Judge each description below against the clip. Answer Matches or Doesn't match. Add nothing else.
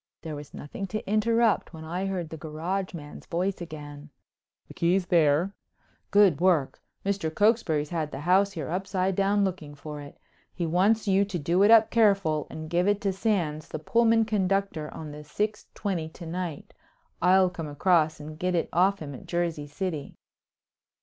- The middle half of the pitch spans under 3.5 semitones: Doesn't match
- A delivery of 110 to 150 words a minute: Doesn't match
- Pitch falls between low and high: Matches